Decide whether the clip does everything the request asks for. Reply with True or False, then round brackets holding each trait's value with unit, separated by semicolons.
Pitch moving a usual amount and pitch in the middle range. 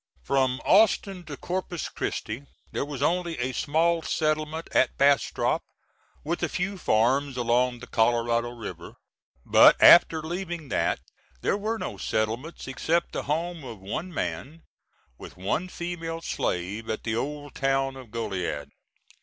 False (5.9 semitones; 145 Hz)